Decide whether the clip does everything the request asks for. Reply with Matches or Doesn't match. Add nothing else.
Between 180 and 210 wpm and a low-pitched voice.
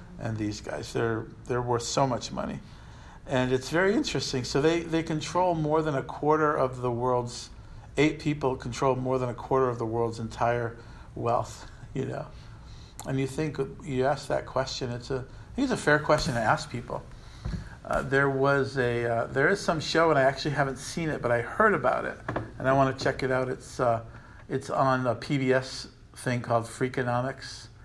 Matches